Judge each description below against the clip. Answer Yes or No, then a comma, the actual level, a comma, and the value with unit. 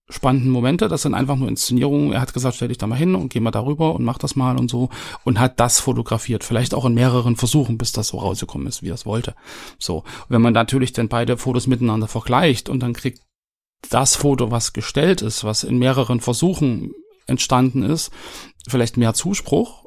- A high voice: No, low, 125 Hz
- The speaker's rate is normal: No, fast, 210 wpm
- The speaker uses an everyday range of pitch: No, narrow, 2.3 semitones